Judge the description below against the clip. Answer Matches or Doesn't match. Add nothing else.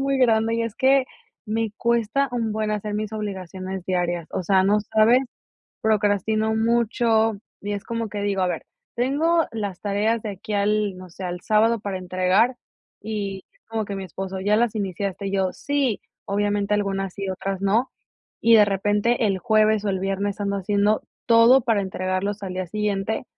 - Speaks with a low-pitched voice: Doesn't match